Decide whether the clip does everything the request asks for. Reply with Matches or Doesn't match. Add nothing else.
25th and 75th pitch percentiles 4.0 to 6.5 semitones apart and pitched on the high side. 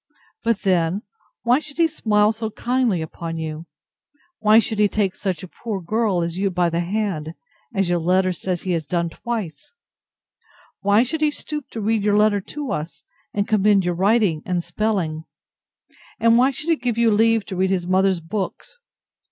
Matches